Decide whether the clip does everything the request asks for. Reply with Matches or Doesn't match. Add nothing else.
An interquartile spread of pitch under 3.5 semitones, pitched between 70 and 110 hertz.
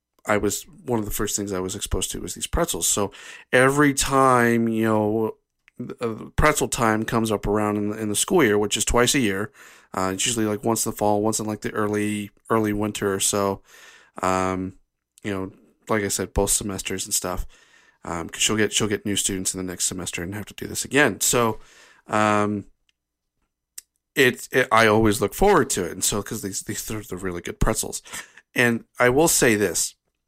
Matches